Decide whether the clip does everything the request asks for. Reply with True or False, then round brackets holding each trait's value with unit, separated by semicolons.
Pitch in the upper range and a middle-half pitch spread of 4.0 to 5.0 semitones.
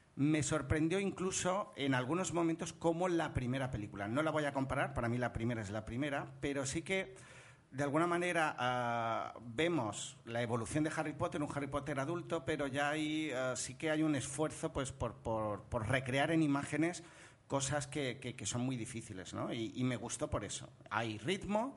False (140 Hz; 4.5 semitones)